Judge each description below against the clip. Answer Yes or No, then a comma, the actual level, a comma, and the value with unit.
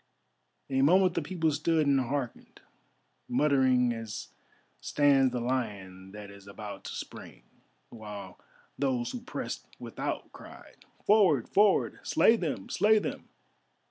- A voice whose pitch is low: Yes, low, 130 Hz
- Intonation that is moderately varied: No, wide, 6.8 semitones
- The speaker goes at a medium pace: No, slow, 125 wpm